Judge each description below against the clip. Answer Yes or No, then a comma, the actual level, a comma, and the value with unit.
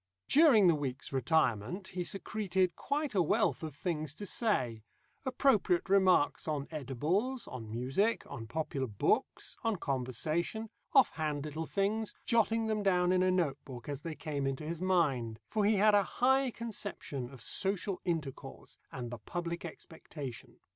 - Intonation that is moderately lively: No, wide, 6.8 semitones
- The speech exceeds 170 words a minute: No, average, 155 wpm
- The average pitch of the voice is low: No, medium, 170 Hz